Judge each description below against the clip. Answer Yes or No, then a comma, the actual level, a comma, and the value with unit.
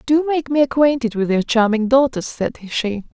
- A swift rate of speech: No, average, 190 wpm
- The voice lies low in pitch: No, very high, 250 Hz